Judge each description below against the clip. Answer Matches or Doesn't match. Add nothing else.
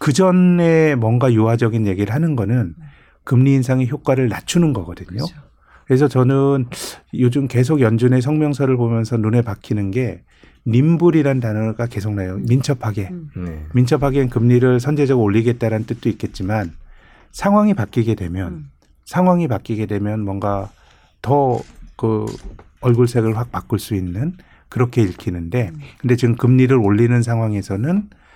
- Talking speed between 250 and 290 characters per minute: Doesn't match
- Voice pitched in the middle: Doesn't match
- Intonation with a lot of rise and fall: Doesn't match